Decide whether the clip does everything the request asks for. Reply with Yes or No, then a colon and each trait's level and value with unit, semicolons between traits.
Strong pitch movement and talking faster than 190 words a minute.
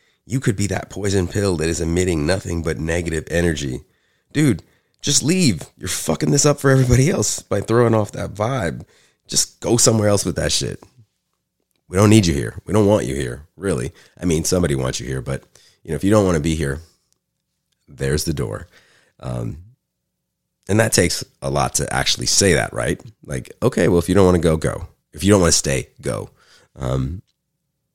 Yes: wide, 5.9 semitones; average, 200 wpm